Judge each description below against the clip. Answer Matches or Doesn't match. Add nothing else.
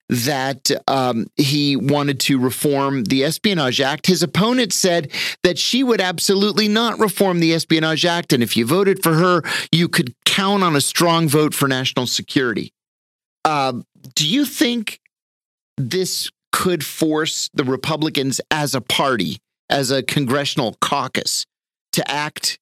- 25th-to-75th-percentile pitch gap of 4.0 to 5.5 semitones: Matches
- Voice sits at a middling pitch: Matches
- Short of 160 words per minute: Matches